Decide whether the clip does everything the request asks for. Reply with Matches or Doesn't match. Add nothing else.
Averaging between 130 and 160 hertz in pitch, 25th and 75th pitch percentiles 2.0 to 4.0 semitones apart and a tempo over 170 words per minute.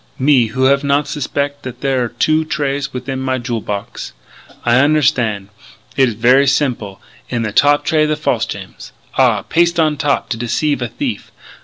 Matches